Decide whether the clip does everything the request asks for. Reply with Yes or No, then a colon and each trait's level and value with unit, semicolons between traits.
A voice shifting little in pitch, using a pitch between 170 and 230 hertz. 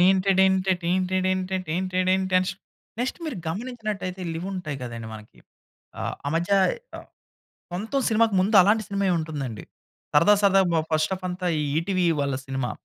No: average, 3.2 semitones; medium, 185 Hz